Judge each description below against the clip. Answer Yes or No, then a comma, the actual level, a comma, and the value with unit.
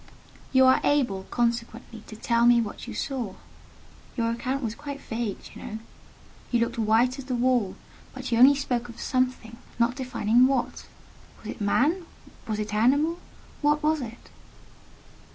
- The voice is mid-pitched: No, high, 240 Hz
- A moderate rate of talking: Yes, average, 170 wpm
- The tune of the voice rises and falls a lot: No, narrow, 2.4 semitones